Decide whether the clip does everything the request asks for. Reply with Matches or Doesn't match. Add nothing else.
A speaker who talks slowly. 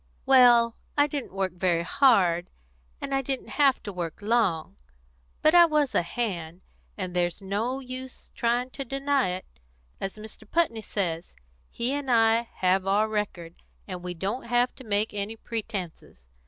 Doesn't match